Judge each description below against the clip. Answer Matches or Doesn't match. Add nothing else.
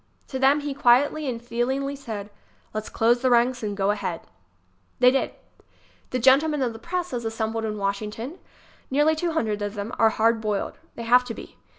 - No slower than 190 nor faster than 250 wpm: Matches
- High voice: Matches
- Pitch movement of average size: Matches